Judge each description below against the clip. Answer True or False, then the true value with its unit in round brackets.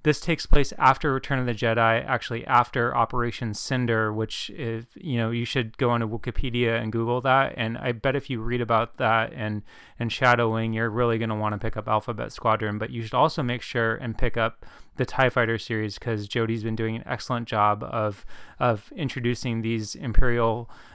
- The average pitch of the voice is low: True (115 Hz)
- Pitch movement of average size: False (1.8 semitones)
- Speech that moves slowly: False (205 wpm)